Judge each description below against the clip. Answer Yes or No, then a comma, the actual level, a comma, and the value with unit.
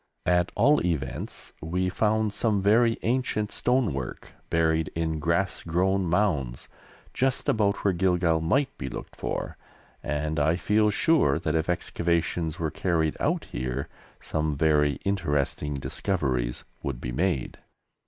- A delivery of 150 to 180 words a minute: No, slow, 135 wpm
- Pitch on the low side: Yes, very low, 85 Hz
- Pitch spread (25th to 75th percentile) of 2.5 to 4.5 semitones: No, average, 5.0 semitones